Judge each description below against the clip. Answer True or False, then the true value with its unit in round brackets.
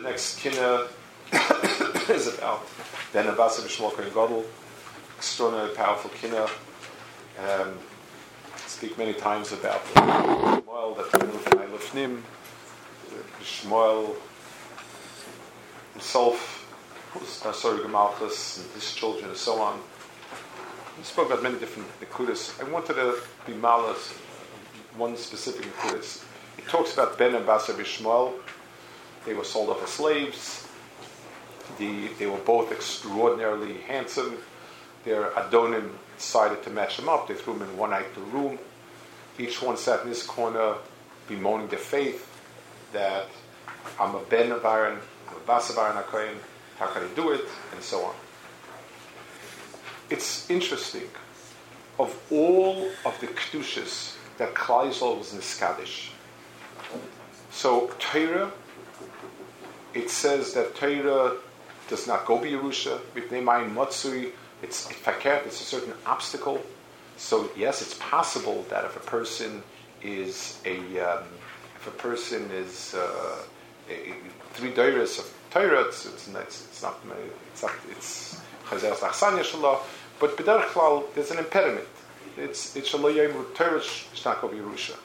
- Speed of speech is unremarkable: False (130 wpm)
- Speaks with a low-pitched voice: True (125 Hz)